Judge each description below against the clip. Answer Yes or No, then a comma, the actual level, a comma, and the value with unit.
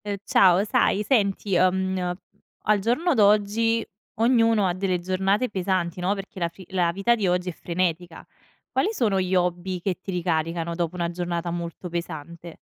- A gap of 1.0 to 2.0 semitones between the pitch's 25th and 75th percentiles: No, average, 2.7 semitones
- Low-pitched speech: No, medium, 185 Hz